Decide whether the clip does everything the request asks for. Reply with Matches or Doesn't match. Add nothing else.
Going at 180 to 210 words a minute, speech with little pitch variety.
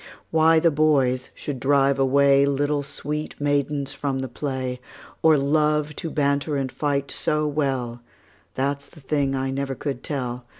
Doesn't match